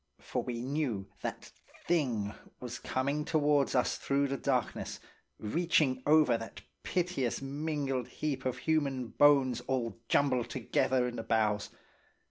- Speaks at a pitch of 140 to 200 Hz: No, low, 130 Hz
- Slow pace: Yes, slow, 130 wpm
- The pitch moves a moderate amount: Yes, average, 3.1 semitones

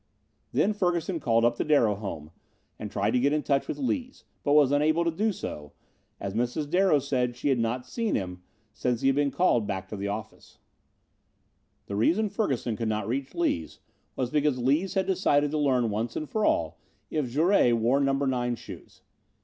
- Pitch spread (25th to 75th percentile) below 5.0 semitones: No, average, 5.3 semitones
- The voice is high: No, low, 135 Hz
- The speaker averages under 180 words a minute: No, average, 195 wpm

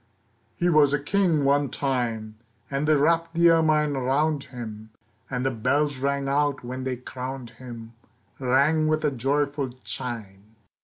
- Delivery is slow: No, average, 150 wpm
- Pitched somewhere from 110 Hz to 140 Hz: Yes, low, 135 Hz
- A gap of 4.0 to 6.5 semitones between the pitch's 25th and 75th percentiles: No, average, 3.2 semitones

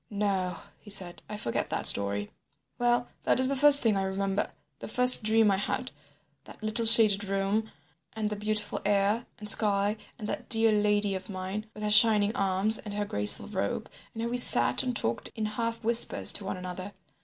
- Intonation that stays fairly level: Yes, narrow, 2.3 semitones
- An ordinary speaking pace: Yes, average, 195 wpm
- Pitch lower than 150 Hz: No, high, 210 Hz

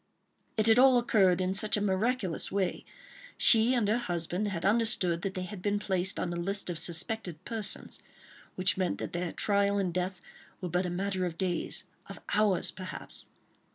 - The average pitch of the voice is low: No, high, 190 Hz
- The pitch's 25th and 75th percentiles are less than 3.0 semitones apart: Yes, narrow, 2.6 semitones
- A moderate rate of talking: Yes, average, 180 wpm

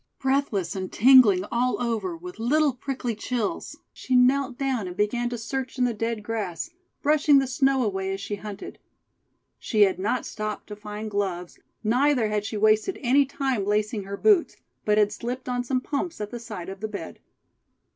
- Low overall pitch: No, high, 230 Hz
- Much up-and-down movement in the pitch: No, average, 4.1 semitones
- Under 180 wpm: No, average, 185 wpm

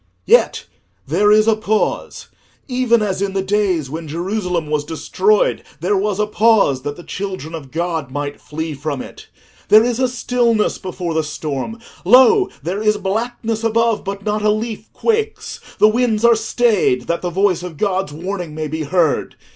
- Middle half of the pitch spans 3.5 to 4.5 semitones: No, average, 5.2 semitones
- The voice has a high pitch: Yes, high, 200 Hz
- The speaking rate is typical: Yes, average, 170 wpm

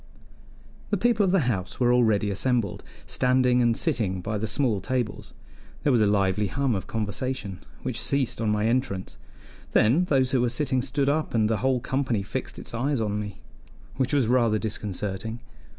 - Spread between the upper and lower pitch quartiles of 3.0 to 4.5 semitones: Yes, average, 3.8 semitones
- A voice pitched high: No, low, 120 Hz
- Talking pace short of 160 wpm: No, average, 180 wpm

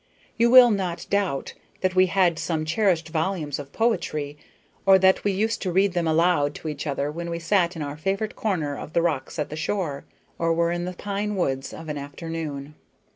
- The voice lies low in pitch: No, medium, 170 Hz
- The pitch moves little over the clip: No, average, 4.1 semitones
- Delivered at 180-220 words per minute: Yes, fast, 205 wpm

